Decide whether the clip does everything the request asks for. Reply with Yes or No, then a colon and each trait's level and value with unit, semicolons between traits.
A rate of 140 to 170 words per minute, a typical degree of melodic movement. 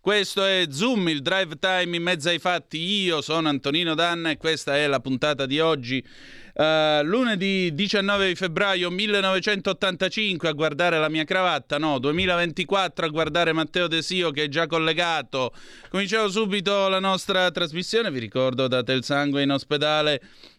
Yes: average, 155 wpm; average, 3.9 semitones